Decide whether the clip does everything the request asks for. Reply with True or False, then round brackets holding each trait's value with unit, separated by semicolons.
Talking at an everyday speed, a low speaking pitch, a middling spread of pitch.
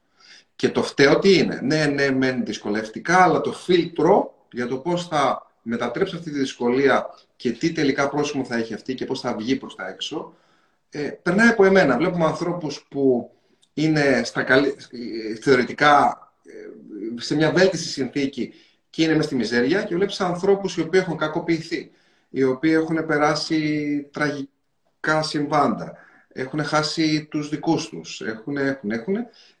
False (150 wpm; 150 Hz; 3.5 semitones)